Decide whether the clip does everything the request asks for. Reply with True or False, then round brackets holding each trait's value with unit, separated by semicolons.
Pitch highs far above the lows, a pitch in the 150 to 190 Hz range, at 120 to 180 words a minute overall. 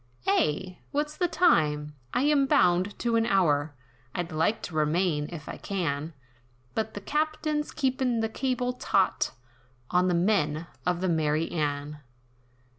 True (8.2 semitones; 185 Hz; 145 wpm)